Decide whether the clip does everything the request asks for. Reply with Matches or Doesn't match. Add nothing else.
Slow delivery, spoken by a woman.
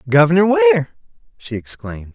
Doesn't match